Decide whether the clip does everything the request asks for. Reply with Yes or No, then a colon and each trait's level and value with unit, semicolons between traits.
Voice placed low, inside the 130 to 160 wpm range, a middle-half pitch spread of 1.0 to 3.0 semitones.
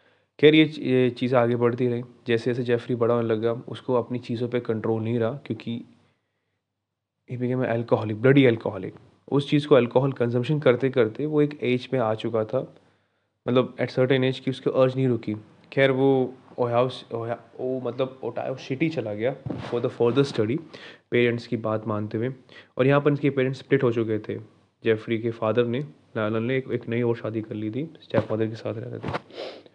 No: low, 120 Hz; fast, 190 wpm; narrow, 2.5 semitones